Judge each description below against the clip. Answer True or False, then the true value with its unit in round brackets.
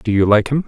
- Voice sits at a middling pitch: False (115 Hz)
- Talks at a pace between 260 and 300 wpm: False (360 wpm)